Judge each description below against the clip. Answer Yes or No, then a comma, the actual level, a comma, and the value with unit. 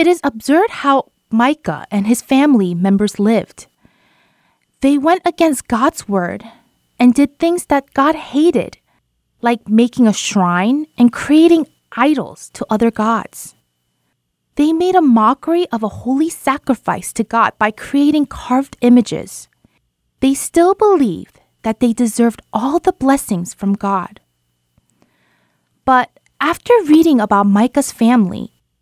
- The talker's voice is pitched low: No, high, 245 Hz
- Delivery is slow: Yes, slow, 130 wpm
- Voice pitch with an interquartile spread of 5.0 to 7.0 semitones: Yes, average, 5.3 semitones